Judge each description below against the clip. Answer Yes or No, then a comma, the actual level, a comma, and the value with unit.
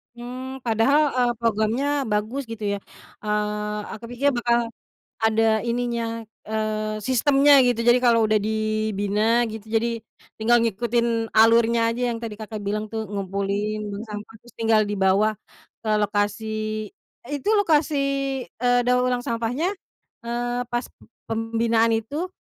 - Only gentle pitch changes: Yes, narrow, 2.0 semitones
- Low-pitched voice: No, high, 225 Hz